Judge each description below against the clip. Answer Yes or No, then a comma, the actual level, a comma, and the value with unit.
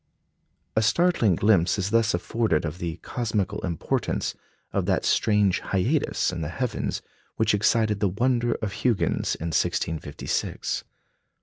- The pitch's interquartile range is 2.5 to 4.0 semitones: No, average, 4.5 semitones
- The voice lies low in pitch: Yes, low, 105 Hz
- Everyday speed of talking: No, slow, 130 wpm